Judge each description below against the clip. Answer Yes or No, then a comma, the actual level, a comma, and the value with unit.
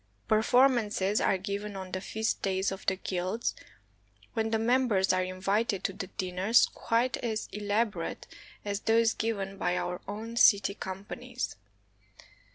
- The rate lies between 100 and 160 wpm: Yes, average, 140 wpm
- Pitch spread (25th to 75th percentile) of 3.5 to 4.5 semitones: No, average, 2.9 semitones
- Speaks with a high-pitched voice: Yes, high, 205 Hz